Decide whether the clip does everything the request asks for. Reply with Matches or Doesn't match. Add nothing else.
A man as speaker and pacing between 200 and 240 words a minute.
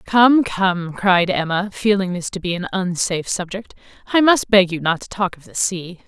Doesn't match